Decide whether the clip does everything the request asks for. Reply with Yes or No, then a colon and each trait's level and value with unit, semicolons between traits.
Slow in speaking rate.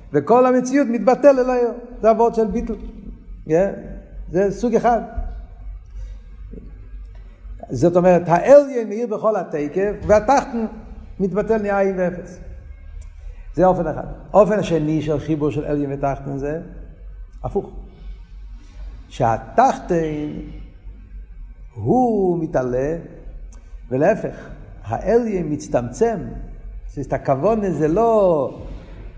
Yes: slow, 95 wpm